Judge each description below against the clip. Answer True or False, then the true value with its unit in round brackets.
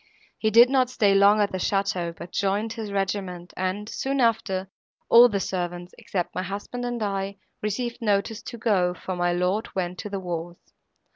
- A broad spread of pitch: False (3.2 semitones)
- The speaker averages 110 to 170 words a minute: False (185 wpm)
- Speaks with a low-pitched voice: False (200 Hz)